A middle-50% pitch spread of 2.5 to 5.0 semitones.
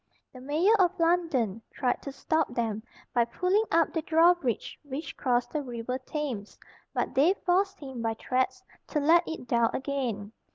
No: wide, 5.4 semitones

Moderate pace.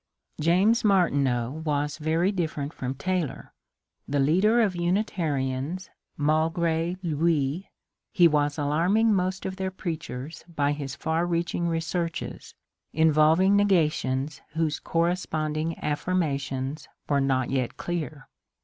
No: slow, 115 wpm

